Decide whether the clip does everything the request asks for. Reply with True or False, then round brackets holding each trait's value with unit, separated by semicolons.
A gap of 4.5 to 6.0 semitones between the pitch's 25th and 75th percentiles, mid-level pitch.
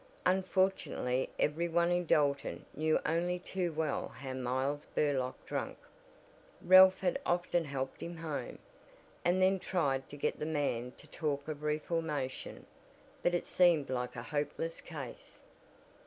False (3.9 semitones; 155 Hz)